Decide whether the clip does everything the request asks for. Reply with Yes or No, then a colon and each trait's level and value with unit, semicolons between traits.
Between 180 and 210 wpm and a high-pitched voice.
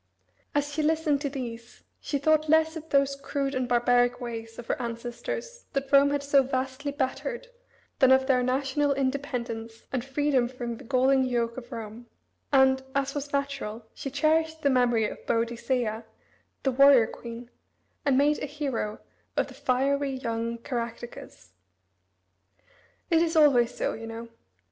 No: average, 155 wpm; very high, 265 Hz